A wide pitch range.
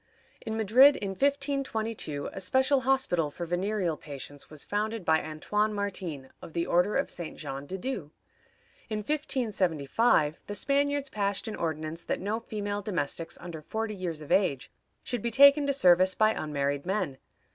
Yes: wide, 6.1 semitones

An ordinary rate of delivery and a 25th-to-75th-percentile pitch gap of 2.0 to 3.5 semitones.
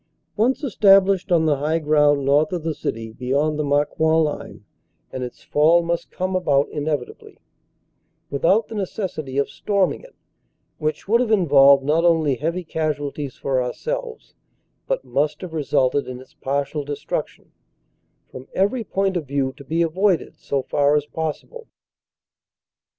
No: average, 155 wpm; average, 4.6 semitones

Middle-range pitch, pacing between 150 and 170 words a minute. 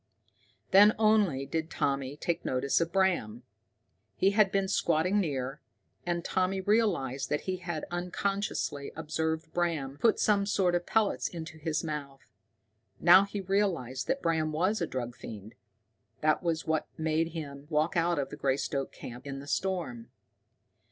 Yes: medium, 160 Hz; average, 155 wpm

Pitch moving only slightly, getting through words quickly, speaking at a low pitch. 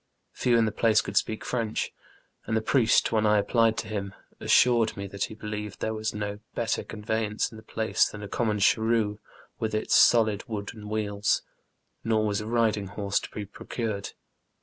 No: narrow, 1.3 semitones; average, 185 wpm; low, 110 Hz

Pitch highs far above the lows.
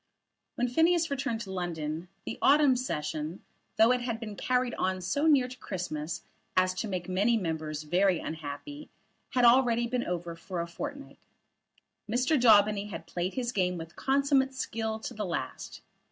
Yes: wide, 6.3 semitones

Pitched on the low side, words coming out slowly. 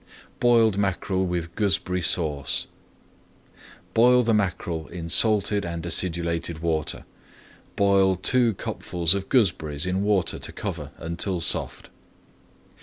Yes: very low, 90 Hz; slow, 110 wpm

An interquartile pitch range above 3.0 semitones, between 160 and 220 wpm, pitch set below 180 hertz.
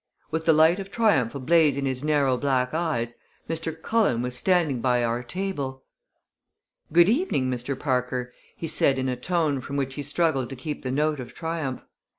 Yes: average, 4.2 semitones; average, 180 wpm; medium, 140 Hz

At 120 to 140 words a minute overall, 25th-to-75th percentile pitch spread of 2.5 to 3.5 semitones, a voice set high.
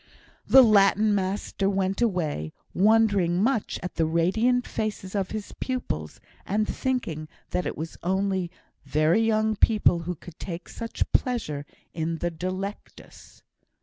No: slow, 135 wpm; average, 4.2 semitones; high, 195 Hz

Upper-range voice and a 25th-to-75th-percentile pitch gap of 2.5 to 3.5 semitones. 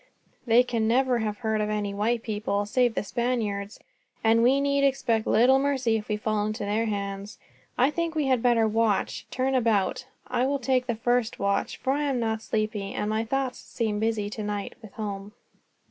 Yes: high, 225 Hz; average, 3.1 semitones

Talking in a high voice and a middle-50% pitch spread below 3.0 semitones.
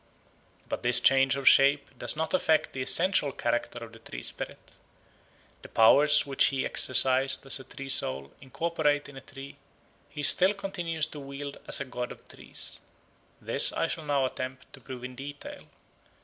No: low, 135 Hz; narrow, 2.4 semitones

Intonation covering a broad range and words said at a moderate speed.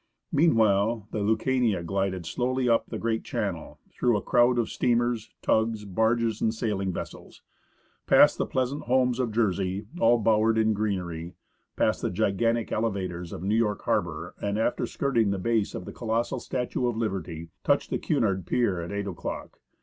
No: average, 3.3 semitones; average, 165 wpm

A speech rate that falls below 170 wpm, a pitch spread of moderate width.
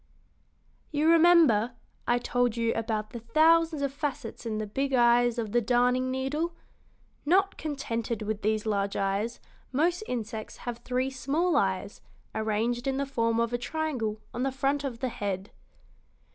Yes: average, 160 wpm; average, 3.9 semitones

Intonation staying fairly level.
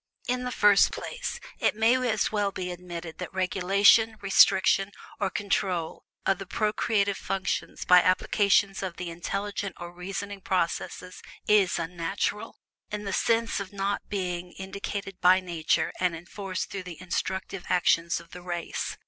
Yes: narrow, 2.1 semitones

